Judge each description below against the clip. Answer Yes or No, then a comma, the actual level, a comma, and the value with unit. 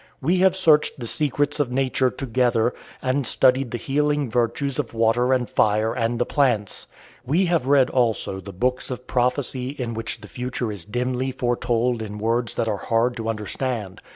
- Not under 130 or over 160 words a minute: No, average, 180 wpm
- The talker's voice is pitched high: No, low, 125 Hz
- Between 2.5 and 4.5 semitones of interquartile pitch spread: Yes, average, 2.8 semitones